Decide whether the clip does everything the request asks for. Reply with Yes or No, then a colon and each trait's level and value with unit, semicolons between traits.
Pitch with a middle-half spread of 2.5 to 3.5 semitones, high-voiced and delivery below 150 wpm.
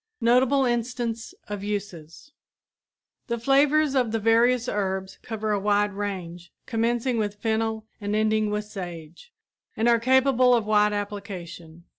Yes: average, 2.8 semitones; high, 215 Hz; slow, 135 wpm